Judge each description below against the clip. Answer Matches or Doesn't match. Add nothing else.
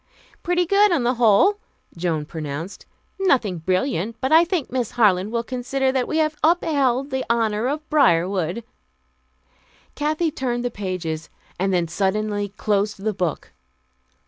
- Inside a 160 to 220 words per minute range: Doesn't match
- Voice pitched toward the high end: Matches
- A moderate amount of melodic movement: Doesn't match